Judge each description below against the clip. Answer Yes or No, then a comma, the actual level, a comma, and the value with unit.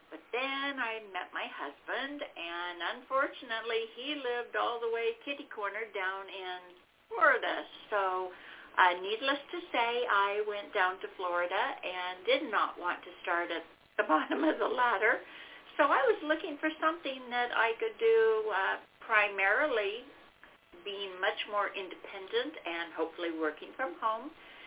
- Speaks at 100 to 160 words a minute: Yes, average, 150 wpm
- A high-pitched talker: Yes, high, 220 Hz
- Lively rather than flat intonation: Yes, wide, 7.4 semitones